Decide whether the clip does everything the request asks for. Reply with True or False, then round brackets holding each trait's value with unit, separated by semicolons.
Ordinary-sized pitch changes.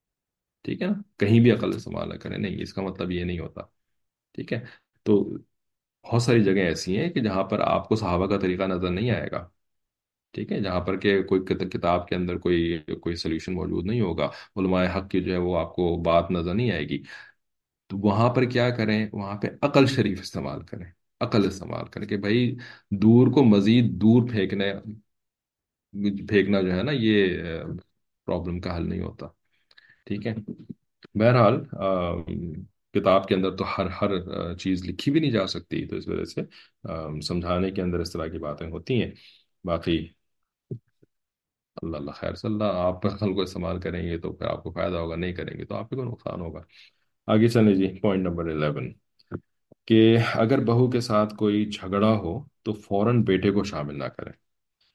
True (3.7 semitones)